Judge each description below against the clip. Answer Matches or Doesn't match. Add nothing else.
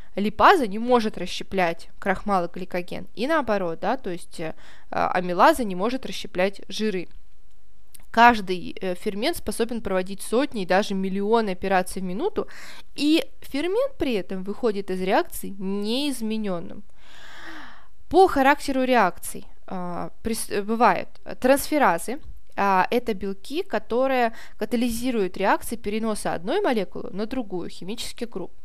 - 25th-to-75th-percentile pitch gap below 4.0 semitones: Doesn't match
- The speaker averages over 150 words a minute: Doesn't match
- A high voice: Matches